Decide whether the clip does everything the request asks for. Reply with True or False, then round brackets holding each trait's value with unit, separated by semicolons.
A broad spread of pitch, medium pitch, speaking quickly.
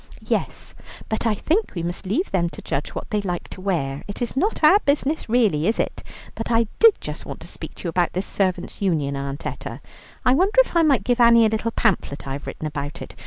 False (6.9 semitones; 205 Hz; 240 wpm)